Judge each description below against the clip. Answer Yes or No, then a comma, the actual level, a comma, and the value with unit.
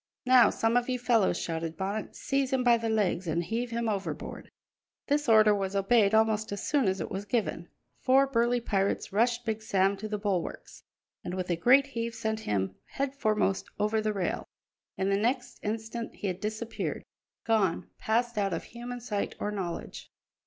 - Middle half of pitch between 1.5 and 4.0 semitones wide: Yes, average, 3.4 semitones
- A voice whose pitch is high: Yes, high, 220 Hz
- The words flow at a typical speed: Yes, average, 180 wpm